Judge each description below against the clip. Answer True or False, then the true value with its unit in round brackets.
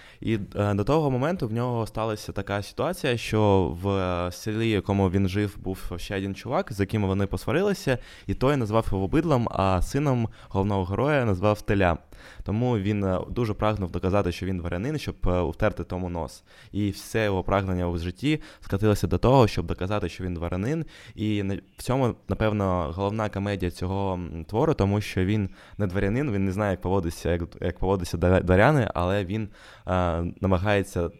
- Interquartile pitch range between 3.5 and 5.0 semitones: False (3.1 semitones)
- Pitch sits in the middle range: False (100 Hz)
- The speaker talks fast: True (165 wpm)